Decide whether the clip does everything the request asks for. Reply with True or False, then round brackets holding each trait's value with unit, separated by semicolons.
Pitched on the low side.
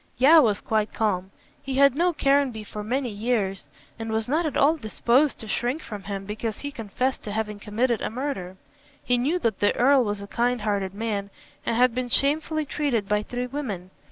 False (235 Hz)